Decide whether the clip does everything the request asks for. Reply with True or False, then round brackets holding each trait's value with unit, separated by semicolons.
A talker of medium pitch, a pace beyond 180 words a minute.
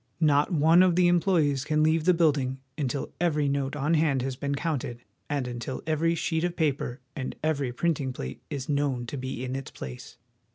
True (145 Hz; 195 wpm)